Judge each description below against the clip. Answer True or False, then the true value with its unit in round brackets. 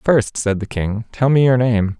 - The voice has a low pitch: True (115 Hz)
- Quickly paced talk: True (240 wpm)